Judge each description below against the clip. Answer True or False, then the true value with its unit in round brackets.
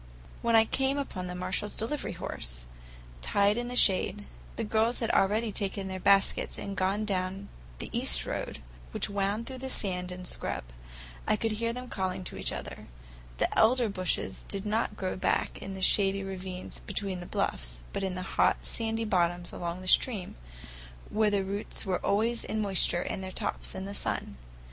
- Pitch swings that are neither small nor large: True (3.1 semitones)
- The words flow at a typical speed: True (185 wpm)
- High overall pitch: True (195 Hz)